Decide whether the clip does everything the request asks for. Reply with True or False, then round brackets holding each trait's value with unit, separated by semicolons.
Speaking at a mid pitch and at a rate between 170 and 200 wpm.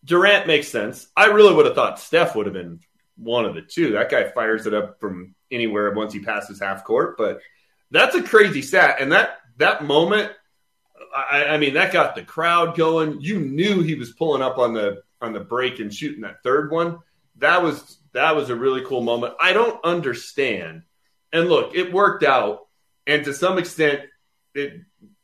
True (145 Hz; 195 wpm)